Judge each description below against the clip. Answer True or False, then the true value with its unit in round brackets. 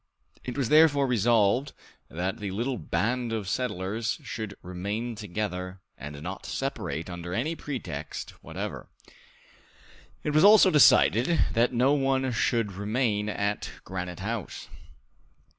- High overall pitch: False (110 Hz)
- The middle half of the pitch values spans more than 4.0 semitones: True (5.0 semitones)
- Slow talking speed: True (125 wpm)